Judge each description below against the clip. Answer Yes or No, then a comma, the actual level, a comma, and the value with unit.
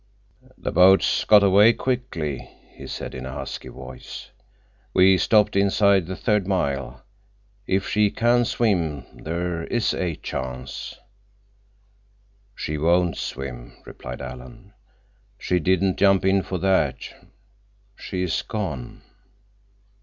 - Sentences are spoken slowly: Yes, slow, 115 wpm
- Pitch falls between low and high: No, very low, 90 Hz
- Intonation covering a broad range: Yes, wide, 5.9 semitones